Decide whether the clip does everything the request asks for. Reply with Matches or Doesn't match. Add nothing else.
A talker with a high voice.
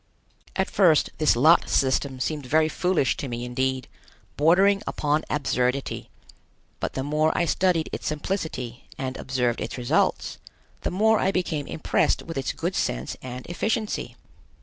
Doesn't match